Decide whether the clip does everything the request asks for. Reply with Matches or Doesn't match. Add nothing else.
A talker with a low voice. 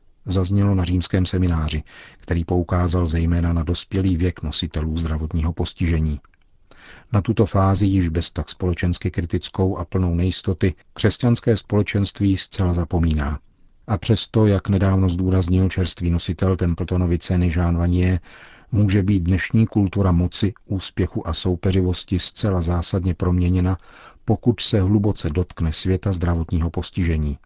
Matches